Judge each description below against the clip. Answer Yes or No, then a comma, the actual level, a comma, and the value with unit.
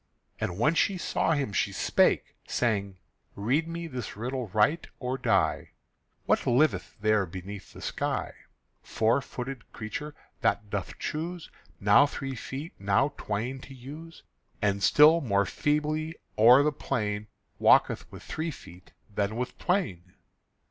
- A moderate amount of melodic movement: No, wide, 6.6 semitones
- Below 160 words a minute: Yes, average, 140 wpm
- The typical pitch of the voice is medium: No, low, 125 Hz